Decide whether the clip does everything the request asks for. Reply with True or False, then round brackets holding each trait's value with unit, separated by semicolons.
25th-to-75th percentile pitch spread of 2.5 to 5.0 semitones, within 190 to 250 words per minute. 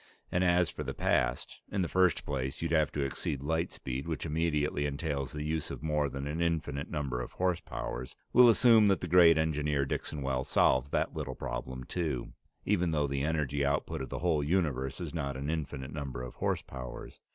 True (3.4 semitones; 200 wpm)